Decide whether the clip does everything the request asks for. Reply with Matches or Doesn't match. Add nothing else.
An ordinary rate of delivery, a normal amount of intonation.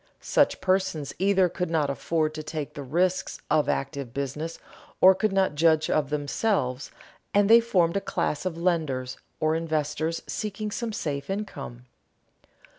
Matches